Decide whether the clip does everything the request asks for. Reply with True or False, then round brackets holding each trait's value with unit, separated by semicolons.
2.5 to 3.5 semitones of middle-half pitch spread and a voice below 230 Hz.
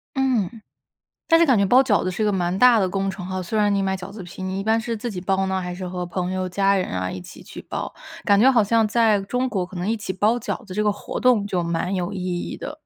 True (3.2 semitones; 195 Hz)